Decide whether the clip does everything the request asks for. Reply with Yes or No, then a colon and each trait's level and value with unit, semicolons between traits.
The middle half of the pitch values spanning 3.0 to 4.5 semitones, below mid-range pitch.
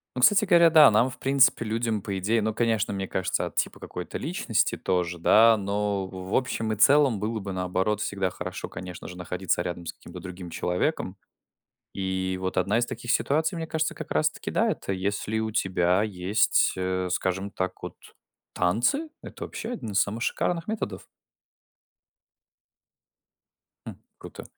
Yes: average, 4.2 semitones; low, 105 Hz